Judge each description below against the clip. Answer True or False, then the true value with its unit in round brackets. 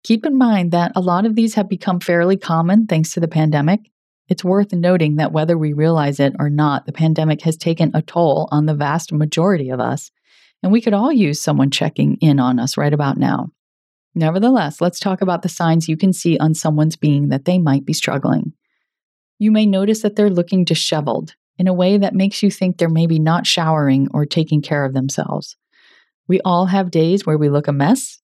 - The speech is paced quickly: True (210 wpm)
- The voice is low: False (165 Hz)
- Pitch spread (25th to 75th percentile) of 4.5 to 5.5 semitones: False (4.0 semitones)